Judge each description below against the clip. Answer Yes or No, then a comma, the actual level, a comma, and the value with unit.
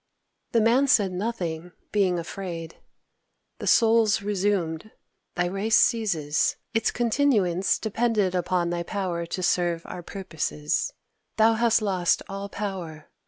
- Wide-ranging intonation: No, average, 4.0 semitones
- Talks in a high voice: Yes, high, 195 Hz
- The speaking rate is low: Yes, slow, 120 wpm